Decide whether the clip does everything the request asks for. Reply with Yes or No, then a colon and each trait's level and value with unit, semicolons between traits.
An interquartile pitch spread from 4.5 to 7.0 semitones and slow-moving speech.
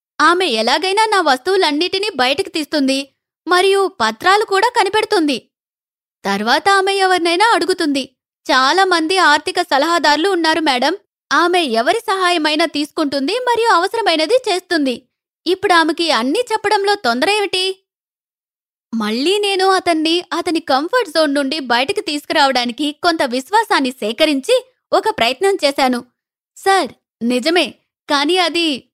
No: average, 5.2 semitones; average, 105 wpm